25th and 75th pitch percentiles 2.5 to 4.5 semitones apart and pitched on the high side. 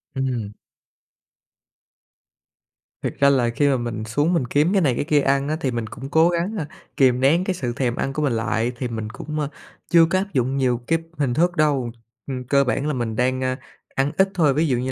No: average, 3.8 semitones; low, 135 Hz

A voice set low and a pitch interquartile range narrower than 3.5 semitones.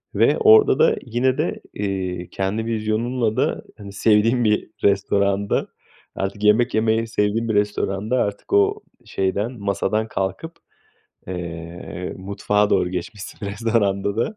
Yes: low, 105 Hz; average, 2.7 semitones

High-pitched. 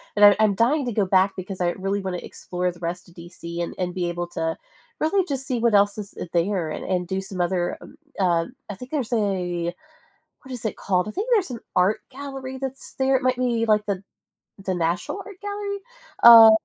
Yes: high, 200 Hz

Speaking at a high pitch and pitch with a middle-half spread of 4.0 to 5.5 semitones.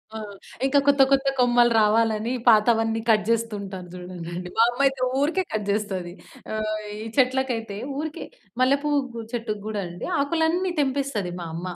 Yes: high, 230 Hz; average, 4.5 semitones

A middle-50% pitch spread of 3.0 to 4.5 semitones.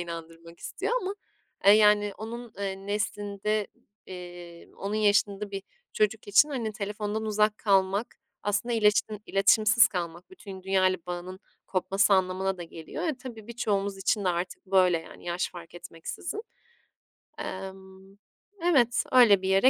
No: narrow, 2.4 semitones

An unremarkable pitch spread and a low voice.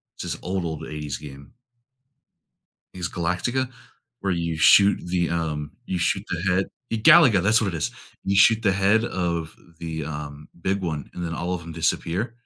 Yes: average, 3.6 semitones; very low, 85 Hz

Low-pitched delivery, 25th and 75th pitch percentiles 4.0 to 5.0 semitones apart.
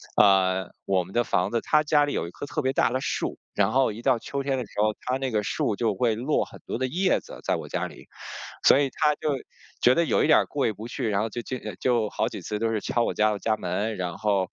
Yes: low, 115 Hz; average, 4.3 semitones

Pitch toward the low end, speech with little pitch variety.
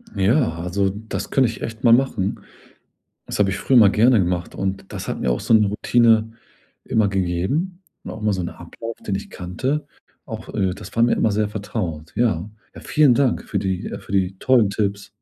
No: low, 105 Hz; average, 3.4 semitones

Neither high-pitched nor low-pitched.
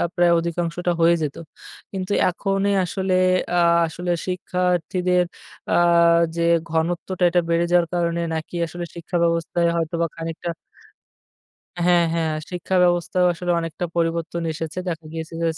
Yes: medium, 170 Hz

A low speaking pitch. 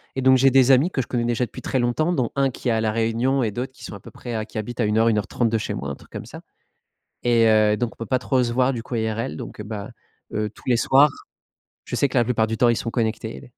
Yes: low, 120 Hz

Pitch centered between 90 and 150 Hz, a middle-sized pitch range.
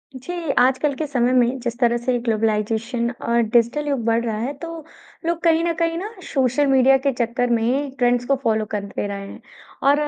No: high, 245 Hz; average, 3.5 semitones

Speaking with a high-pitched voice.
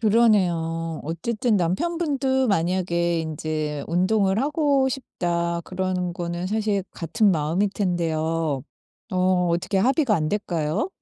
No: medium, 180 Hz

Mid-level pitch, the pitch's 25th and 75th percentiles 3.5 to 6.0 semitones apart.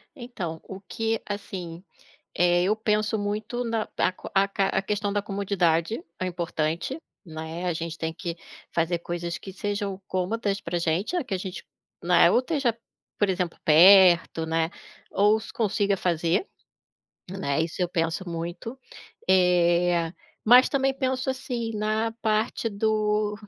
No: high, 195 Hz; average, 3.9 semitones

